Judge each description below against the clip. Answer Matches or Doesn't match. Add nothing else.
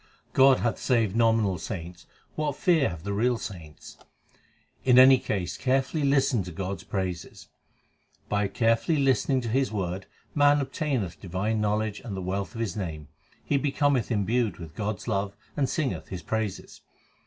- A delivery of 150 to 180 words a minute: Matches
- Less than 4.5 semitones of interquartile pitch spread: Doesn't match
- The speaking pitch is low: Matches